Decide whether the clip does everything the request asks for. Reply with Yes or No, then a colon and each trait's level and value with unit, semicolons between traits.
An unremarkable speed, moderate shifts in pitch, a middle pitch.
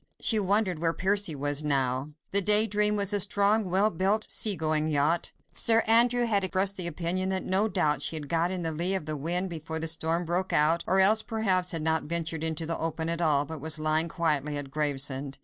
No: fast, 220 wpm; average, 4.1 semitones; medium, 170 Hz